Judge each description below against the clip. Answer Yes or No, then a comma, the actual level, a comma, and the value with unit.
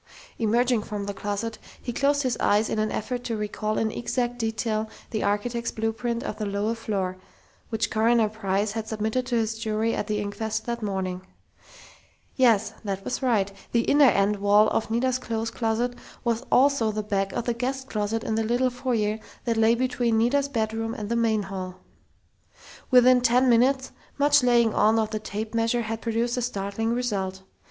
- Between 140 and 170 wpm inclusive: No, average, 180 wpm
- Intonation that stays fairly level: Yes, narrow, 2.3 semitones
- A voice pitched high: Yes, high, 225 Hz